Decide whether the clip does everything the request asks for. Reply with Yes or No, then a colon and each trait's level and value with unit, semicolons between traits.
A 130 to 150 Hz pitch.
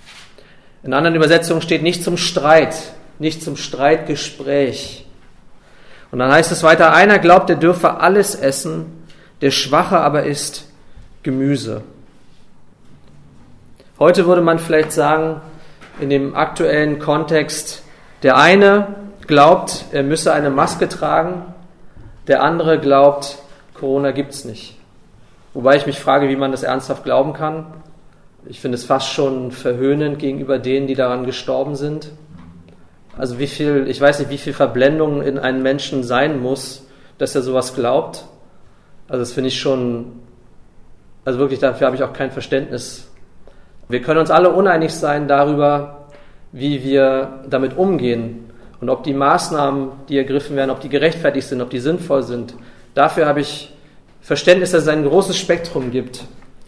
Yes: medium, 140 Hz